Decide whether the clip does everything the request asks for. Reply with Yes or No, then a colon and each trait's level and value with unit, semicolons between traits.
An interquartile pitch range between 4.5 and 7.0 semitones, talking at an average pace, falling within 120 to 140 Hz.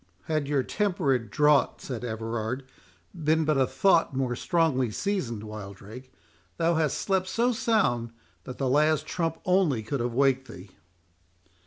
Yes: wide, 5.5 semitones; average, 145 wpm; low, 135 Hz